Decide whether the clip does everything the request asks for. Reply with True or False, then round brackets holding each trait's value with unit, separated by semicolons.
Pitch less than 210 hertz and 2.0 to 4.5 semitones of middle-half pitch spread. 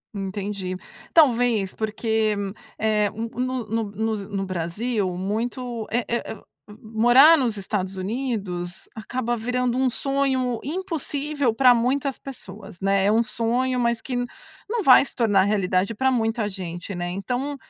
False (225 Hz; 4.1 semitones)